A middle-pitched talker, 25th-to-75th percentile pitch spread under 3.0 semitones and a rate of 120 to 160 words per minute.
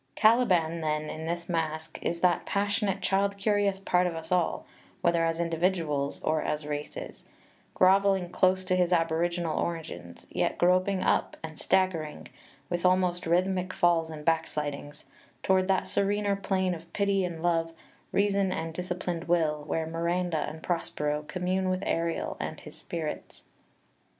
Yes: medium, 175 Hz; narrow, 2.5 semitones; average, 150 wpm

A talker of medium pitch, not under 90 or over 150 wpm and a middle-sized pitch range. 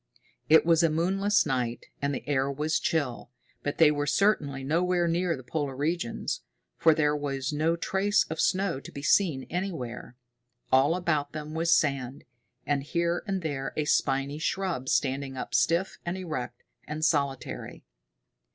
No: medium, 150 Hz; average, 160 wpm; average, 3.7 semitones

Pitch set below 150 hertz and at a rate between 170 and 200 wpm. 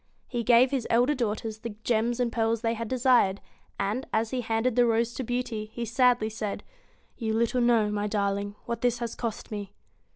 No: high, 230 Hz; average, 195 wpm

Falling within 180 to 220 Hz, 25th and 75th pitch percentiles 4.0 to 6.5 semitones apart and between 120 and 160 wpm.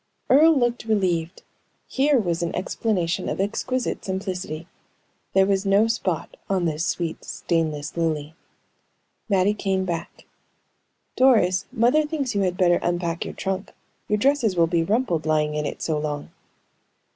Yes: medium, 185 Hz; average, 4.8 semitones; average, 145 wpm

